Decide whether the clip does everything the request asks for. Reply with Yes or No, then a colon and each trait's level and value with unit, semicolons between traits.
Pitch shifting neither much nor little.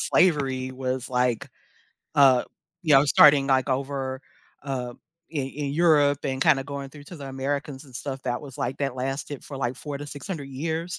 No: narrow, 1.6 semitones